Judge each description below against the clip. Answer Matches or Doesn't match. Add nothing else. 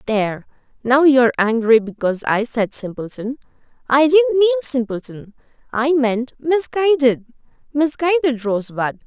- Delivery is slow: Matches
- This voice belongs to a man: Doesn't match